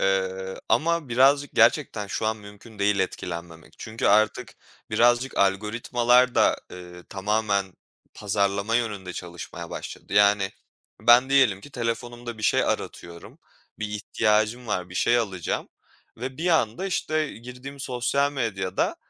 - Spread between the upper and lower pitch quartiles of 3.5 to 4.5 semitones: Yes, average, 4.0 semitones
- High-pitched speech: No, low, 110 Hz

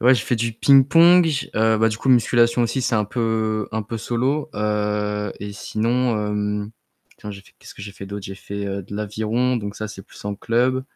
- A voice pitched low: Yes, low, 110 Hz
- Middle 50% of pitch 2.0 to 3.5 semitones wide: Yes, average, 2.8 semitones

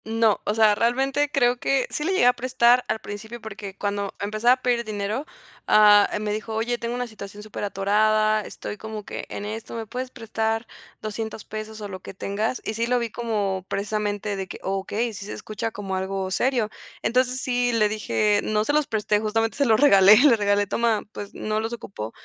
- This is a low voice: No, high, 215 Hz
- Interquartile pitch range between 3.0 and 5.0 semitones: No, narrow, 2.5 semitones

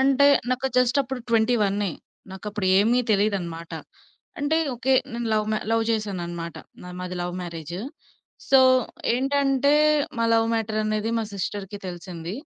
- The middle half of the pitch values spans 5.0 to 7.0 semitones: Yes, average, 5.3 semitones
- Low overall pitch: No, high, 215 Hz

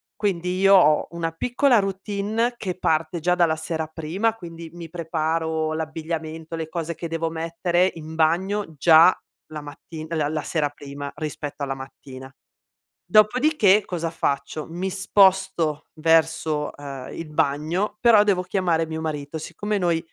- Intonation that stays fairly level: No, average, 3.1 semitones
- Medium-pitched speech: Yes, medium, 165 Hz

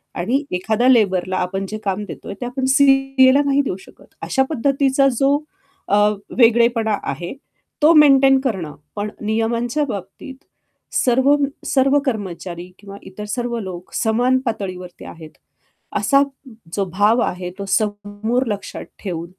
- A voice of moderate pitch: No, high, 225 Hz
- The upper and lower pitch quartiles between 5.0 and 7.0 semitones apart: Yes, wide, 5.4 semitones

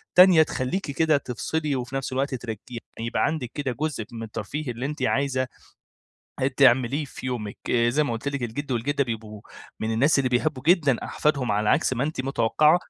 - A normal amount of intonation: Yes, average, 3.7 semitones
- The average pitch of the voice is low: Yes, low, 130 Hz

